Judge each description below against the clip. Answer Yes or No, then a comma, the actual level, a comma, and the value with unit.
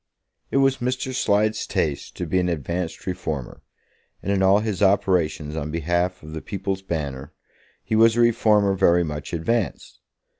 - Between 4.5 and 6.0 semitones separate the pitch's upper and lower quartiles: Yes, average, 5.1 semitones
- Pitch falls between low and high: No, very low, 95 Hz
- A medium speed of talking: Yes, average, 160 wpm